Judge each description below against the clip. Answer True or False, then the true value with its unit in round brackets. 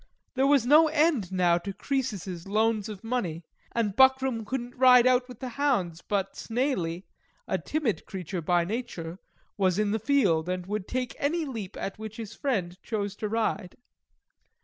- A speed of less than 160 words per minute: False (170 wpm)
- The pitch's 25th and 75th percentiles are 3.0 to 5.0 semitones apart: False (5.5 semitones)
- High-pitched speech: True (220 Hz)